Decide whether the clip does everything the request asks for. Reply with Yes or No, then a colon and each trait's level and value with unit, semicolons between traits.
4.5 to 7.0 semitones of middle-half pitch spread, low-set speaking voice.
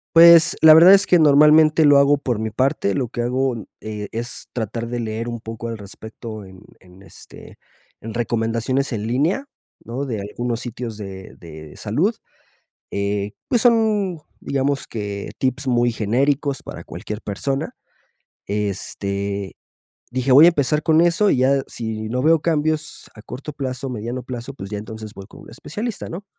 Yes: average, 5.0 semitones; low, 120 Hz